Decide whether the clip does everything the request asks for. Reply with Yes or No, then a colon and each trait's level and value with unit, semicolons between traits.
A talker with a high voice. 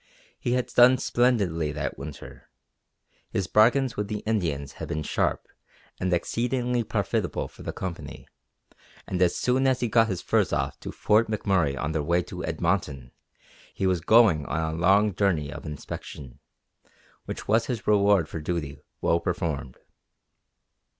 No: very low, 90 Hz